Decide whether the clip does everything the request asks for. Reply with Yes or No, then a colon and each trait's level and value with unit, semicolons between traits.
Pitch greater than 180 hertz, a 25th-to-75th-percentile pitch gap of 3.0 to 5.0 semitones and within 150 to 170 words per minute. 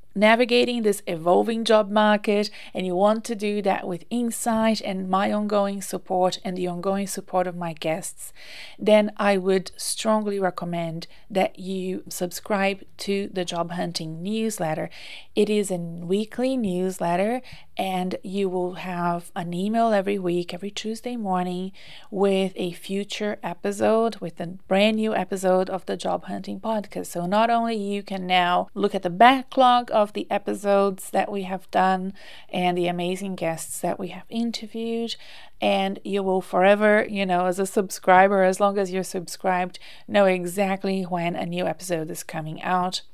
No: high, 190 Hz; narrow, 2.6 semitones; average, 160 wpm